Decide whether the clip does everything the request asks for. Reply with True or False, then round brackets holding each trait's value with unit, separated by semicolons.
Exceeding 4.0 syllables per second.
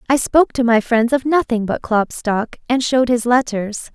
True (4.9 syllables/s)